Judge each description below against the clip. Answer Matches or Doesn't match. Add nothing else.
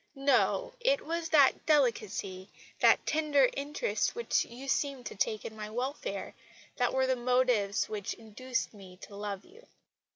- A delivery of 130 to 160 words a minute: Matches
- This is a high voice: Matches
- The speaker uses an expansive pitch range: Matches